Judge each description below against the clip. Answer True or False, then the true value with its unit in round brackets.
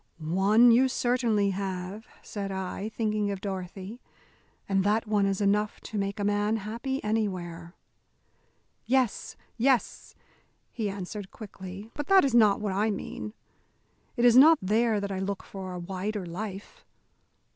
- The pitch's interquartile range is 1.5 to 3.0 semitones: True (2.6 semitones)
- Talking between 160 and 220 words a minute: False (145 wpm)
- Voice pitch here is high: True (205 Hz)